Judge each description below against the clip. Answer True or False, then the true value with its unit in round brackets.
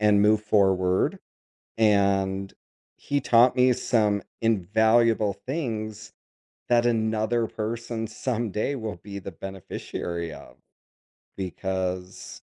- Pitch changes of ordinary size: True (3.0 semitones)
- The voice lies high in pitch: False (105 Hz)